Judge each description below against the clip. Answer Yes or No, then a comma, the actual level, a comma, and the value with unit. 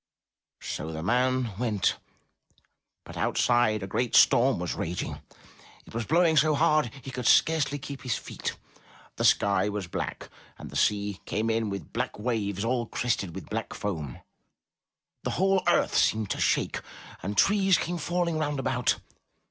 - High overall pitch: No, low, 120 Hz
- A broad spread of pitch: Yes, wide, 6.0 semitones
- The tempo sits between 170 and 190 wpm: No, average, 155 wpm